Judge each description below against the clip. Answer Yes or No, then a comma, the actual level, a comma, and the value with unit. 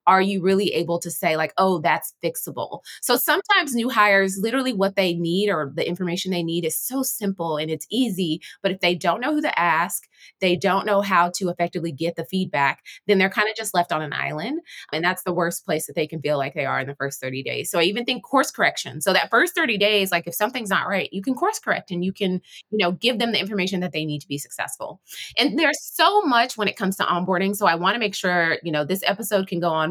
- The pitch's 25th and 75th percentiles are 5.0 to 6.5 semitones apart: No, average, 3.7 semitones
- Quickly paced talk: Yes, fast, 260 wpm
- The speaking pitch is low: No, medium, 185 Hz